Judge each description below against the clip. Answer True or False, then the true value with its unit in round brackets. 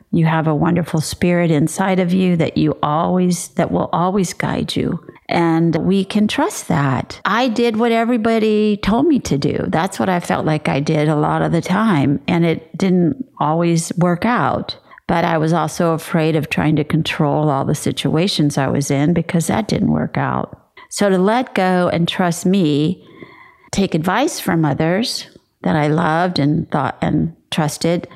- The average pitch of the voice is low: False (170 Hz)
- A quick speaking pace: False (180 wpm)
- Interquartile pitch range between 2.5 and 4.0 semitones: True (3.5 semitones)